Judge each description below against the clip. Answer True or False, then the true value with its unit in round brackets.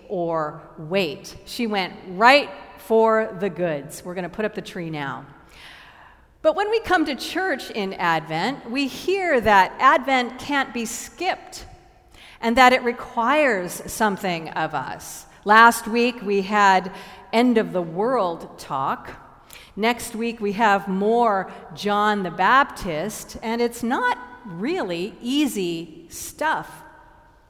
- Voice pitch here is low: False (220 Hz)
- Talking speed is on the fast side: False (135 wpm)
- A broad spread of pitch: False (4.6 semitones)